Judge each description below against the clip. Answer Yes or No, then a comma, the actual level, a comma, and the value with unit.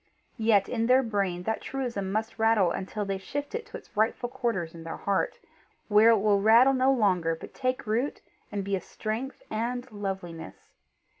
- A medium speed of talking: Yes, average, 180 wpm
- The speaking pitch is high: Yes, high, 215 Hz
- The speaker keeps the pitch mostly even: No, average, 3.9 semitones